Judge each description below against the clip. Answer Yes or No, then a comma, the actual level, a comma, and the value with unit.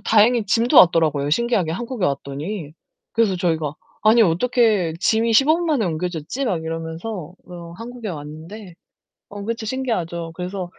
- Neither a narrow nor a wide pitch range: No, wide, 5.8 semitones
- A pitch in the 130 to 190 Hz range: Yes, medium, 185 Hz